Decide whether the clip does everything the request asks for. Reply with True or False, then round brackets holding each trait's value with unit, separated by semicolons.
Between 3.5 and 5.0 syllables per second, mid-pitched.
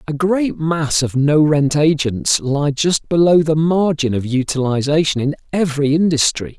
True (4.5 syllables/s; 150 Hz)